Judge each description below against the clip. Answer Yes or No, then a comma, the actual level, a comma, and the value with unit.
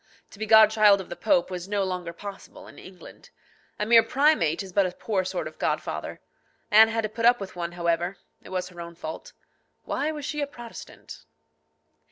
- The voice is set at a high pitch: Yes, high, 200 Hz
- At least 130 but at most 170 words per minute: No, average, 200 wpm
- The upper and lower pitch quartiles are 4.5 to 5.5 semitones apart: No, average, 3.9 semitones